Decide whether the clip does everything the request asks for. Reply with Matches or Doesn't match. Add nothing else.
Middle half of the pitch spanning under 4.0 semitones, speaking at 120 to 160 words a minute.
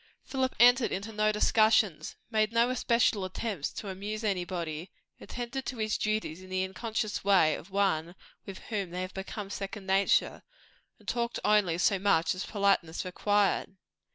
Matches